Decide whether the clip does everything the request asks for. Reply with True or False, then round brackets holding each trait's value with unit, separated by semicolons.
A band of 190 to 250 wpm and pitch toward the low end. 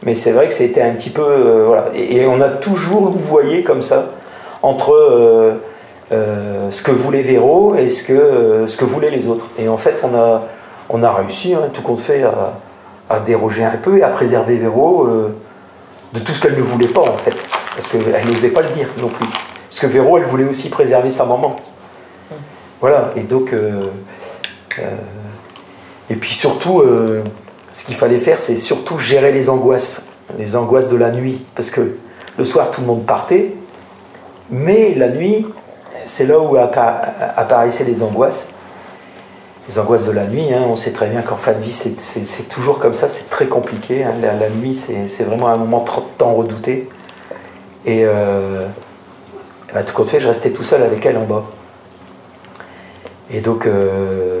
True (195 wpm; 120 Hz)